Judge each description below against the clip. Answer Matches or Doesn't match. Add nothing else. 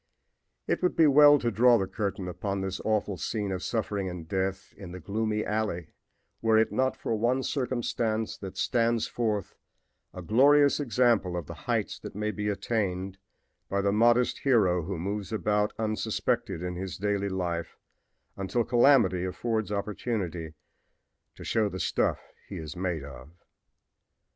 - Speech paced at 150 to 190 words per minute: Matches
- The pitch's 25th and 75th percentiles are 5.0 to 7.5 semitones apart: Doesn't match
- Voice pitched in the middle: Doesn't match